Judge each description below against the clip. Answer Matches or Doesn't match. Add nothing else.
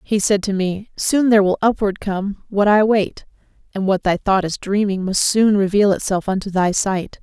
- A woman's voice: Matches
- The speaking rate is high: Matches